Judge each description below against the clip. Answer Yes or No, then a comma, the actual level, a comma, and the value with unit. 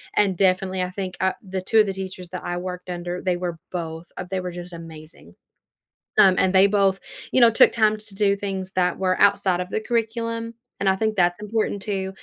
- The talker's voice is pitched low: No, high, 190 Hz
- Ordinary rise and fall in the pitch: No, narrow, 2.1 semitones